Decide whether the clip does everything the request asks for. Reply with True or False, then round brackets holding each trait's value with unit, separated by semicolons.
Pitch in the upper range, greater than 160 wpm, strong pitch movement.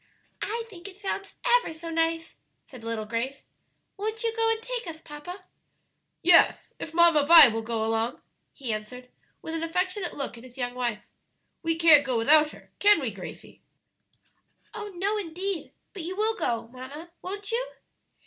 True (330 Hz; 170 wpm; 7.8 semitones)